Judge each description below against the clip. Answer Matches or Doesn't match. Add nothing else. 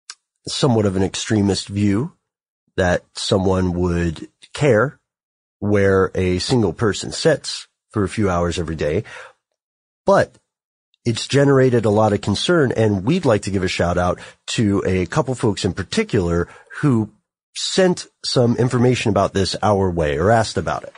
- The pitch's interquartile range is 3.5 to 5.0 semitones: Matches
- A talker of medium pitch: Doesn't match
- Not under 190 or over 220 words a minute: Doesn't match